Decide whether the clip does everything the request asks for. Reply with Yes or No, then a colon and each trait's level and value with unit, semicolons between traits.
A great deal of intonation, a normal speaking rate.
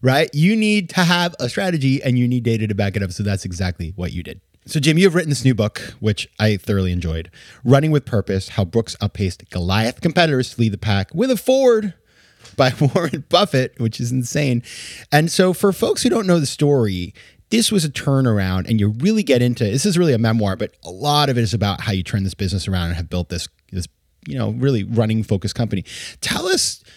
No: wide, 6.8 semitones; fast, 230 wpm